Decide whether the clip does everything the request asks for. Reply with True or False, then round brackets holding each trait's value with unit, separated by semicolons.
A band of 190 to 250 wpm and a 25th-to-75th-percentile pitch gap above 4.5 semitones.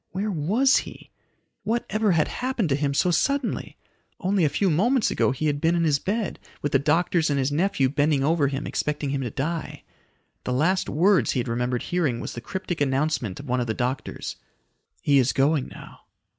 True (200 wpm; 5.3 semitones)